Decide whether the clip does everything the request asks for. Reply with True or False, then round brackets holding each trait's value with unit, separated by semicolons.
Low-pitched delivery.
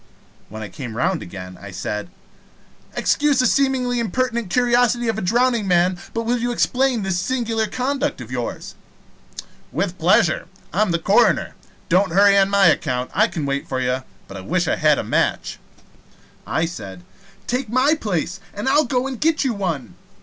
False (205 Hz)